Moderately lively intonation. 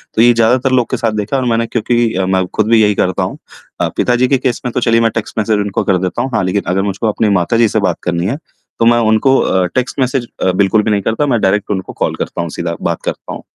Yes: average, 3.3 semitones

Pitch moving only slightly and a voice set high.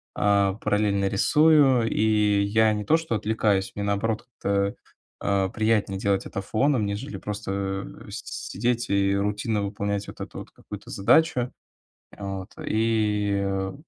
No: narrow, 2.0 semitones; low, 105 Hz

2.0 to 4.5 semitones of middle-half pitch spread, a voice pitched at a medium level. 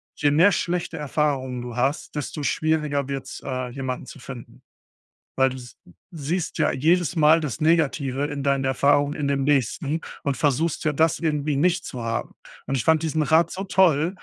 Yes: average, 2.9 semitones; medium, 145 Hz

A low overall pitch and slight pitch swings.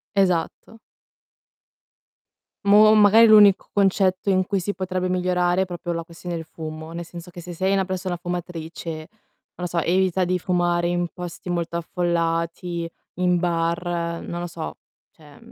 No: medium, 175 Hz; narrow, 1.7 semitones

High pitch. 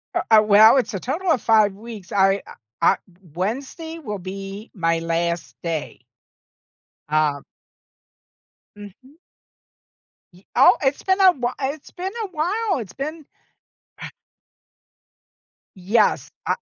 Yes: high, 215 Hz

